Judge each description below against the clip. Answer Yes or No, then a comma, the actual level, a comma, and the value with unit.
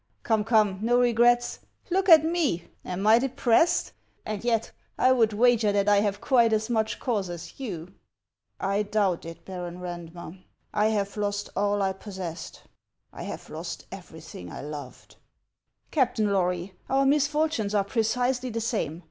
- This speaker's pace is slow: No, average, 170 wpm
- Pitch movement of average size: Yes, average, 4.2 semitones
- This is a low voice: No, high, 215 Hz